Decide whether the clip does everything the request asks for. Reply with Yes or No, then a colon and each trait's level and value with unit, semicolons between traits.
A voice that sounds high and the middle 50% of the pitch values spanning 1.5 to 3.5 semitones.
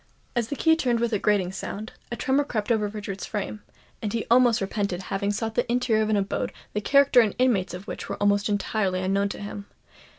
Yes: high, 210 Hz; average, 2.9 semitones